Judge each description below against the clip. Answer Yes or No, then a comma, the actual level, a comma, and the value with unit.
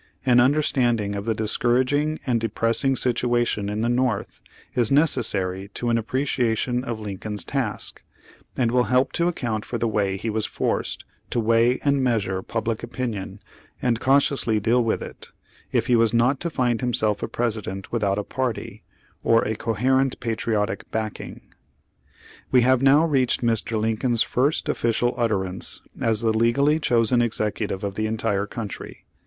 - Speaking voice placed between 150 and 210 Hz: No, low, 115 Hz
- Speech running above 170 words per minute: No, average, 160 wpm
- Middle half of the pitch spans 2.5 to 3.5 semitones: Yes, average, 2.8 semitones